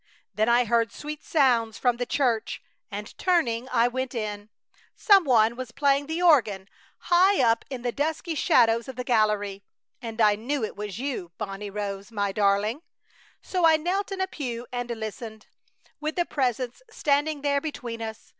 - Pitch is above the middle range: Yes, high, 240 Hz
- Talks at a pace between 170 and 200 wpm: Yes, average, 175 wpm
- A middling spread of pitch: Yes, average, 5.0 semitones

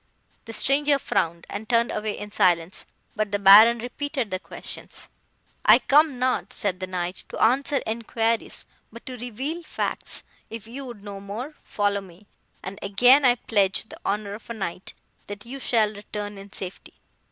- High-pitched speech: Yes, high, 215 Hz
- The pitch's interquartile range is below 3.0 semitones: No, average, 3.6 semitones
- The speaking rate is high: No, average, 170 wpm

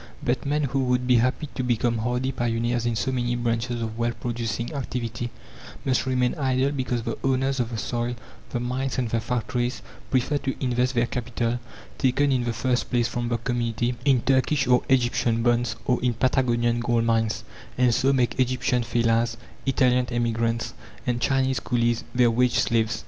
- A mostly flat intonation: Yes, narrow, 1.6 semitones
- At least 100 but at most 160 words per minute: No, average, 175 wpm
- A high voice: No, low, 120 Hz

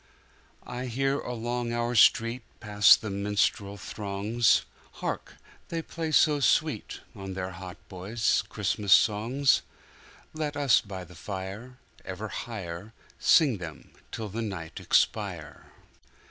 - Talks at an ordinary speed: No, slow, 110 wpm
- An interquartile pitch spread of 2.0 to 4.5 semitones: Yes, average, 3.9 semitones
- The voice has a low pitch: Yes, low, 110 Hz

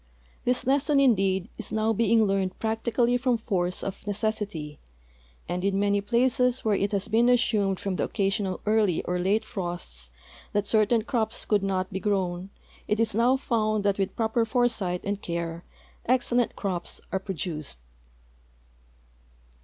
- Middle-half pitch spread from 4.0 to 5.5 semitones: No, average, 3.2 semitones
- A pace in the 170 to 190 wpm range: No, average, 155 wpm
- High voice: Yes, high, 205 Hz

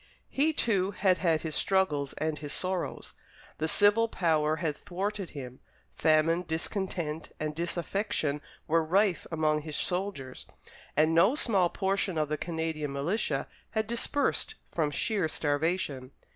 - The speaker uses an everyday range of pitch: Yes, average, 4.1 semitones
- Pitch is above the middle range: No, medium, 165 Hz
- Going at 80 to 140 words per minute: Yes, slow, 135 wpm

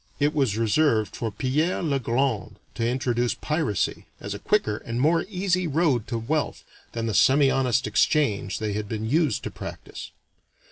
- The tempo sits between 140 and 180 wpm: Yes, average, 160 wpm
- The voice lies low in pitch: Yes, low, 130 Hz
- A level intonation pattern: No, wide, 5.4 semitones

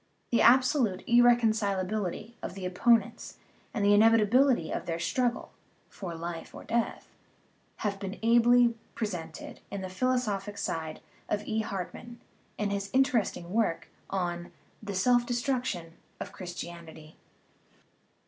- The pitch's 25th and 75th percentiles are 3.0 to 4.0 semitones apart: No, average, 4.6 semitones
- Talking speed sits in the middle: No, slow, 130 wpm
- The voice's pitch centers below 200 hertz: No, high, 205 Hz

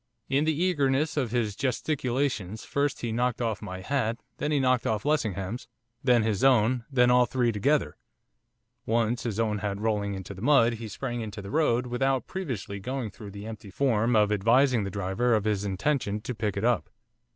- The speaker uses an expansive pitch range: No, average, 4.0 semitones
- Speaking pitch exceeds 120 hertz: No, low, 115 Hz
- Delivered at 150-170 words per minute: No, average, 190 wpm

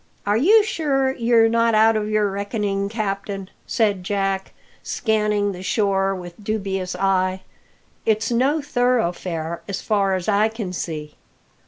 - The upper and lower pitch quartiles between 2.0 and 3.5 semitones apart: Yes, average, 2.8 semitones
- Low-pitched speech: No, high, 205 Hz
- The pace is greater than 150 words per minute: No, average, 145 wpm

